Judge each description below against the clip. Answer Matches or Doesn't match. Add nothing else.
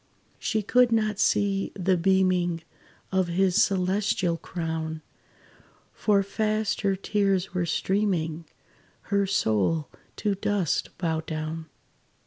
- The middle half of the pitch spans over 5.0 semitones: Doesn't match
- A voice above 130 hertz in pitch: Matches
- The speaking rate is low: Matches